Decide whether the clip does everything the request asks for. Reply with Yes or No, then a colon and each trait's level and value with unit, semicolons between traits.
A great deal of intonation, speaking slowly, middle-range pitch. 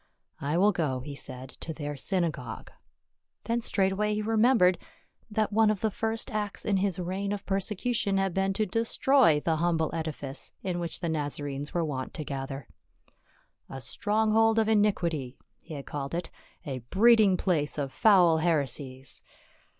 No: wide, 6.2 semitones; average, 170 wpm; medium, 180 Hz